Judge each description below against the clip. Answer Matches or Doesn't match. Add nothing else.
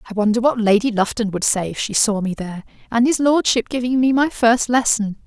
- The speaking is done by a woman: Matches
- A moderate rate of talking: Doesn't match